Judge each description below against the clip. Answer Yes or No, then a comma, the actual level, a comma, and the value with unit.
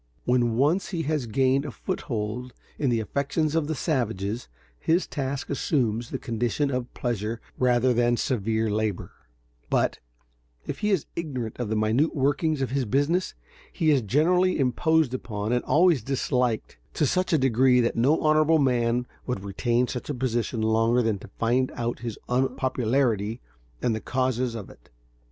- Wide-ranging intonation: No, average, 3.8 semitones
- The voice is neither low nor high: No, low, 125 Hz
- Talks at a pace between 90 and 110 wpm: No, average, 165 wpm